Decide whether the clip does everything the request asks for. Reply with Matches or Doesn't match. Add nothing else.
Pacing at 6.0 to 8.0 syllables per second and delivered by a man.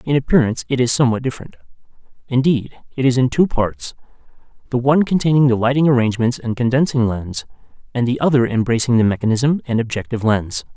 Matches